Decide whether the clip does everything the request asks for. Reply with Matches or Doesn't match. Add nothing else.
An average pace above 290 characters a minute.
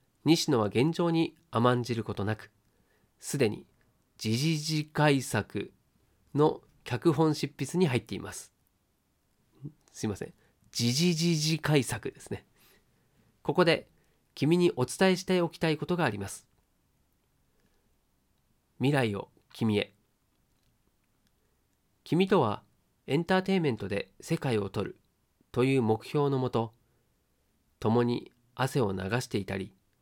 Doesn't match